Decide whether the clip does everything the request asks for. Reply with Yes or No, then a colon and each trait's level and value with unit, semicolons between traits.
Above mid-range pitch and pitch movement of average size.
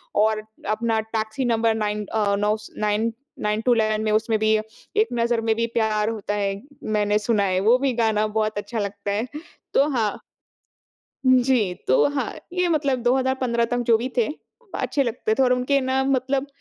Yes: high, 225 Hz; average, 3.1 semitones